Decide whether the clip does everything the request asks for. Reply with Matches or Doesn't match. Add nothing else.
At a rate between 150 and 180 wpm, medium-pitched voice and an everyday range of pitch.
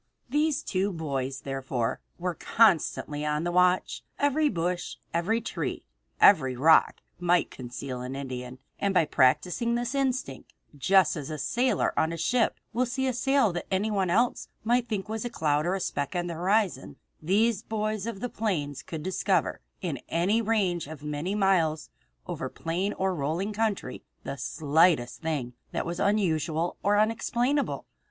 Doesn't match